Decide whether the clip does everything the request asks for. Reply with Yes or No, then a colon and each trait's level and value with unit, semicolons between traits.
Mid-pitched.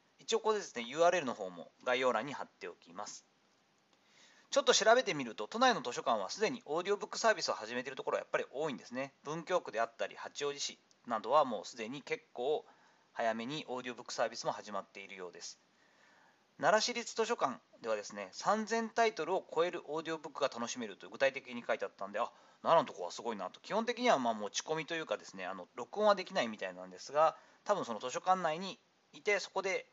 Yes: medium, 175 Hz